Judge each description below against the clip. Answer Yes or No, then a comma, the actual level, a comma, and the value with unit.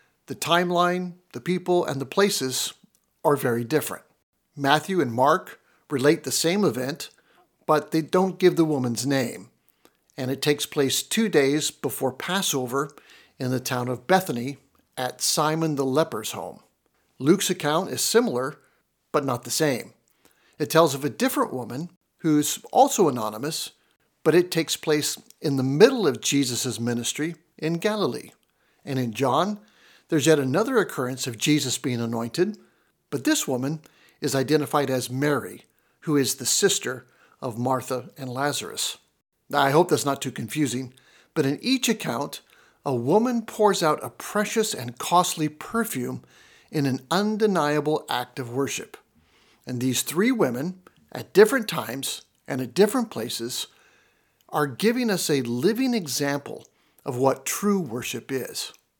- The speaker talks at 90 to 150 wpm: Yes, average, 145 wpm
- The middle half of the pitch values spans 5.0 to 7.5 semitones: Yes, average, 5.3 semitones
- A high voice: No, medium, 150 Hz